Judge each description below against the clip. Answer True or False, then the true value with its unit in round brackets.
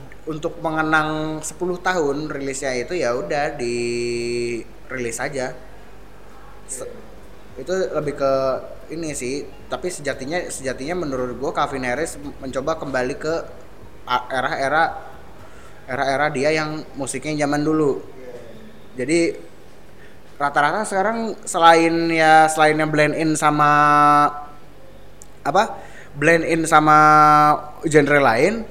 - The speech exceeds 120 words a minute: False (105 wpm)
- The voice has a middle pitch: True (145 Hz)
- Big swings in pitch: False (3.4 semitones)